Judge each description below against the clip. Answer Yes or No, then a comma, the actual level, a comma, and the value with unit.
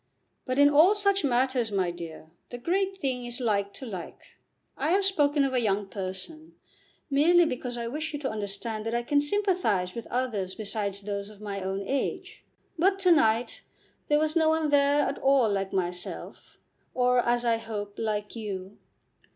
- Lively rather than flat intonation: Yes, wide, 6.3 semitones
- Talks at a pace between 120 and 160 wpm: No, average, 180 wpm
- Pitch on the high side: Yes, high, 240 Hz